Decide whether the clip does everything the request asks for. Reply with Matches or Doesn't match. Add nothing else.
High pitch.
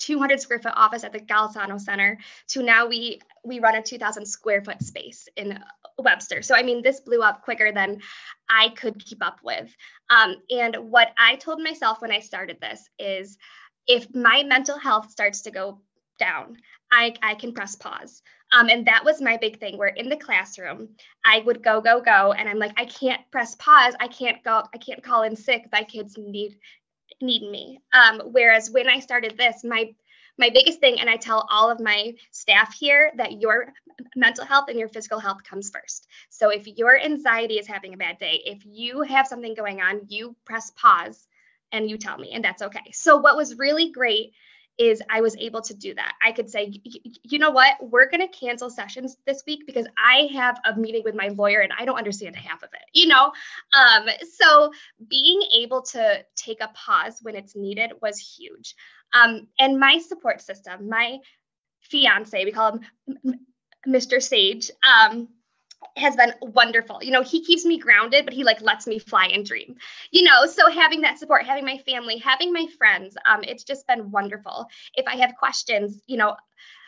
Matches